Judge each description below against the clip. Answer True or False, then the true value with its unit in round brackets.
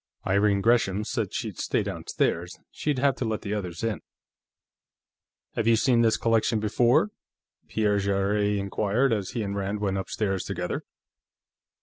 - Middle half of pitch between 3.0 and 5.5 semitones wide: False (2.5 semitones)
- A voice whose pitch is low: True (105 Hz)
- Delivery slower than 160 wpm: True (145 wpm)